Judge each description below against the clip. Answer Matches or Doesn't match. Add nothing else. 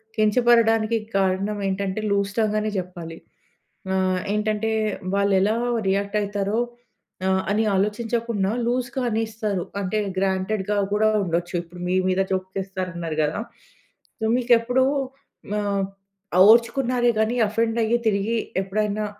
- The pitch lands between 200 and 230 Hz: Matches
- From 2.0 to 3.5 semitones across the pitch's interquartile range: Matches